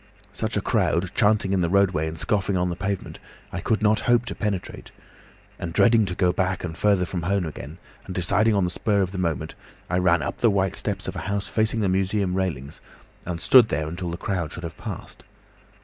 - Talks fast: Yes, fast, 220 wpm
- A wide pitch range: No, average, 2.8 semitones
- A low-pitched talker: Yes, very low, 95 Hz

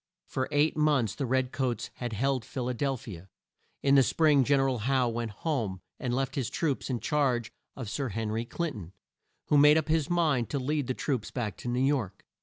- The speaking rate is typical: No, fast, 225 wpm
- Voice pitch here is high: No, low, 130 Hz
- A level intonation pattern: No, average, 3.5 semitones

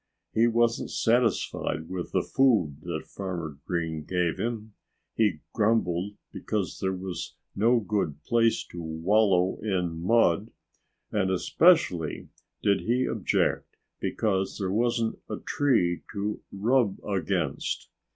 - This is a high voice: No, low, 100 Hz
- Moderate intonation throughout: Yes, average, 4.4 semitones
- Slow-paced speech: Yes, slow, 120 wpm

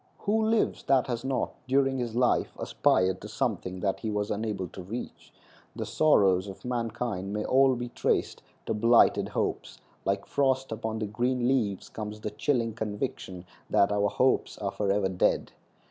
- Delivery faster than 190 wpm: No, average, 165 wpm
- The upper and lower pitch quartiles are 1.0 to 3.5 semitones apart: No, average, 4.0 semitones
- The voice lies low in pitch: Yes, low, 110 Hz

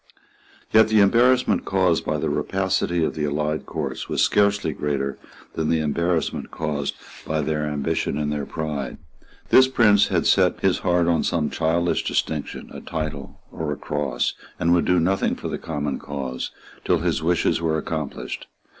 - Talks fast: No, average, 165 wpm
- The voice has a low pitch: Yes, very low, 80 Hz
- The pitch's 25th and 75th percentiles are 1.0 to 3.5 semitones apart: Yes, average, 3.1 semitones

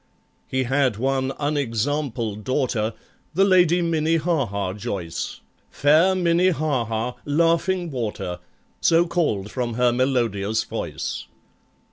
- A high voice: No, low, 135 Hz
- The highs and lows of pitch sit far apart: Yes, wide, 6.4 semitones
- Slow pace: Yes, slow, 105 wpm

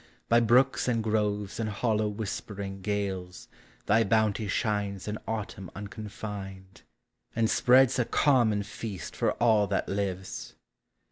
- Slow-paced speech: Yes, slow, 125 wpm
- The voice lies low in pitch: Yes, low, 105 Hz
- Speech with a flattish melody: Yes, narrow, 2.2 semitones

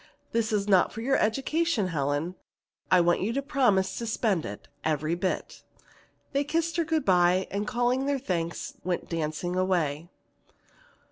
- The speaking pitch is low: No, high, 190 Hz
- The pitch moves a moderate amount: No, wide, 6.8 semitones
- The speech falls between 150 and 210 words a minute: Yes, average, 155 wpm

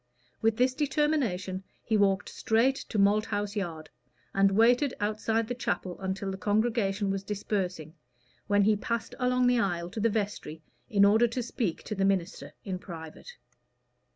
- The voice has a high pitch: Yes, high, 205 Hz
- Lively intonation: No, average, 3.1 semitones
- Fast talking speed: No, average, 155 wpm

